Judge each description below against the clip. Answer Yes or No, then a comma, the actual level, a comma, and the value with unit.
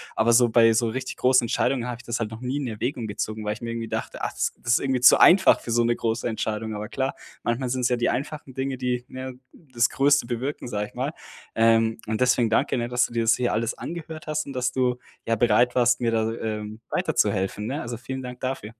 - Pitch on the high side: No, low, 120 Hz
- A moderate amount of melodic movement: No, narrow, 2.3 semitones